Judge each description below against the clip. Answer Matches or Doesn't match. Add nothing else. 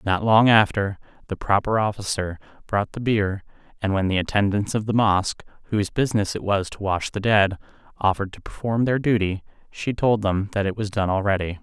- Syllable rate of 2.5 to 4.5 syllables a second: Doesn't match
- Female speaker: Doesn't match